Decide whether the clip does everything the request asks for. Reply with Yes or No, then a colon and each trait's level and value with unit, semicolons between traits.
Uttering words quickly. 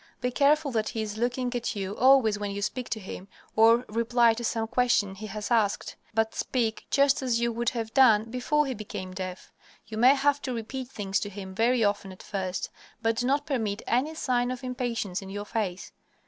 Yes: fast, 210 wpm